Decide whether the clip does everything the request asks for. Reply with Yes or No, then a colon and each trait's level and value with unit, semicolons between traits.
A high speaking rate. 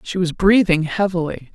No: average, 155 wpm